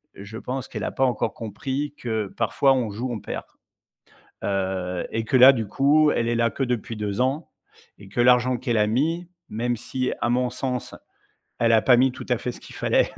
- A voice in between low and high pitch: No, low, 120 Hz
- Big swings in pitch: No, average, 2.9 semitones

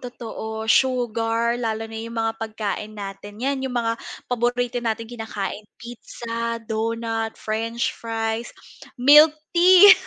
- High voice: Yes, high, 230 Hz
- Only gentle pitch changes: Yes, narrow, 1.6 semitones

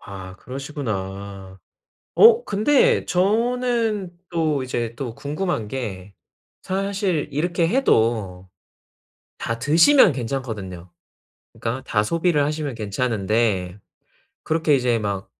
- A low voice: Yes, low, 130 Hz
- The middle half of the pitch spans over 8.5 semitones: Yes, wide, 8.9 semitones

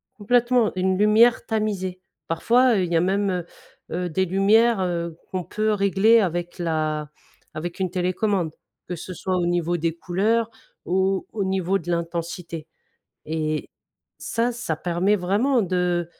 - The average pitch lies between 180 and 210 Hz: Yes, medium, 185 Hz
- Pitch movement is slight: No, average, 3.4 semitones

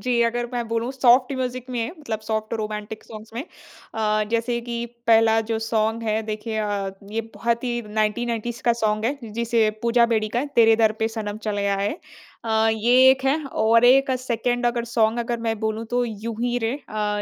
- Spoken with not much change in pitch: Yes, narrow, 1.8 semitones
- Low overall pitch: No, high, 230 Hz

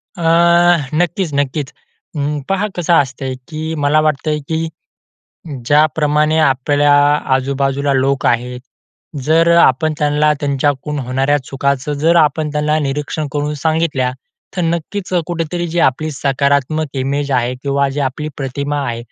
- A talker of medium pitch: Yes, medium, 145 Hz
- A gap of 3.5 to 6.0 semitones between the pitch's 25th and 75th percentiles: No, narrow, 2.4 semitones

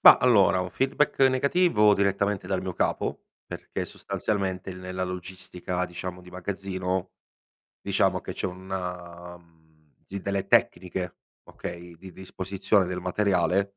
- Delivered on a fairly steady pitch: Yes, narrow, 1.5 semitones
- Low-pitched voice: Yes, very low, 95 Hz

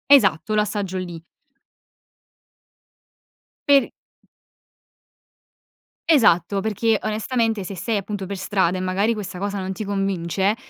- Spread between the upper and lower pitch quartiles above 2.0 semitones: Yes, narrow, 2.5 semitones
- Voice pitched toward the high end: Yes, high, 200 Hz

